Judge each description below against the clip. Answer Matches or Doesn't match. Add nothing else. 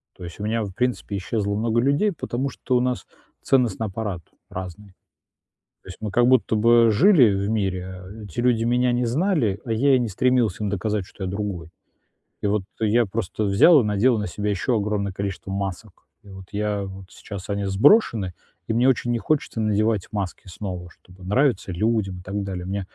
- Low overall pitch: Matches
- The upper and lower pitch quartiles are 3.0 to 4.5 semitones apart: Matches